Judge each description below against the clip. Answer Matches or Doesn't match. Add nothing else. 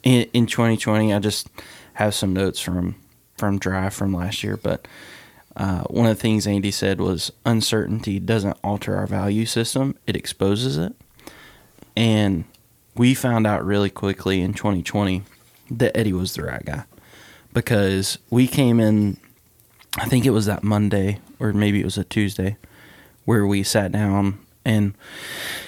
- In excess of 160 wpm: Doesn't match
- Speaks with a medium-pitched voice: Doesn't match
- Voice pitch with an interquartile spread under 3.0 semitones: Matches